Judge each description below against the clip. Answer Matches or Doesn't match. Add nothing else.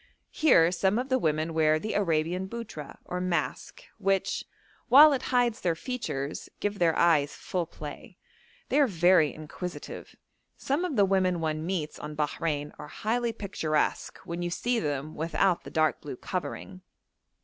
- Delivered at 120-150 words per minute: Doesn't match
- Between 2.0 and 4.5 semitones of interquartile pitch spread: Doesn't match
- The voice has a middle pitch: Matches